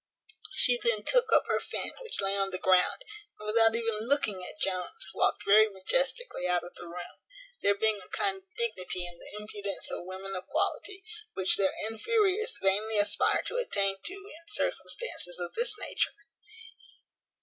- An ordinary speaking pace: Yes, average, 170 wpm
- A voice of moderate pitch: No, high, 210 Hz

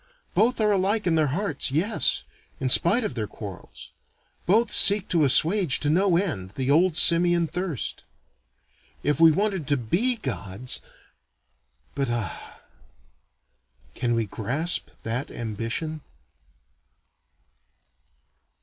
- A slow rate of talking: Yes, slow, 115 wpm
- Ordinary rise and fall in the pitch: No, wide, 7.3 semitones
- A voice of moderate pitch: Yes, medium, 155 Hz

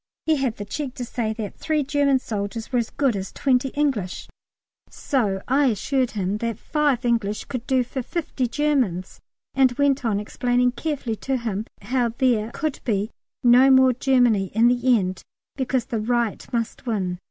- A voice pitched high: Yes, high, 245 Hz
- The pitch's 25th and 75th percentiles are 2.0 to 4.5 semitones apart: Yes, average, 3.5 semitones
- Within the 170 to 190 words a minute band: Yes, average, 175 wpm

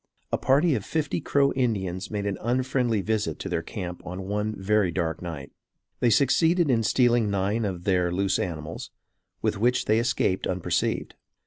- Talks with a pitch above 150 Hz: No, low, 105 Hz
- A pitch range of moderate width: Yes, average, 4.9 semitones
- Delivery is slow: No, average, 165 wpm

